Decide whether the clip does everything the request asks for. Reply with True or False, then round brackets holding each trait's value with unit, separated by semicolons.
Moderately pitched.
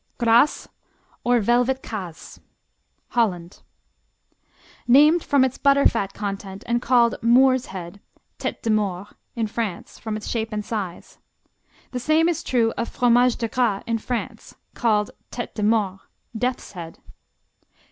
False (230 Hz)